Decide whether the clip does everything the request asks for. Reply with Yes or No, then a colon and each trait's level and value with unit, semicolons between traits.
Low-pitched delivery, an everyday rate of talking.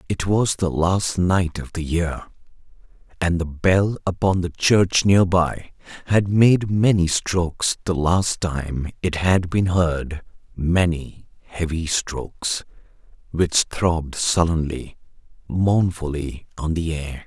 No: very low, 85 Hz; slow, 130 wpm